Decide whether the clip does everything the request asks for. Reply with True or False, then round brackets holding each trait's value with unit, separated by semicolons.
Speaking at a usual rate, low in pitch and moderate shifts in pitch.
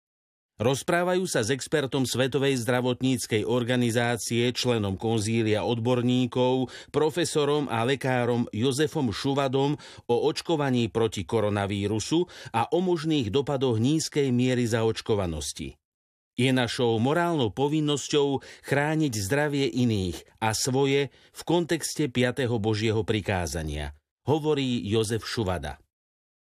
False (95 wpm; 125 Hz; 4.0 semitones)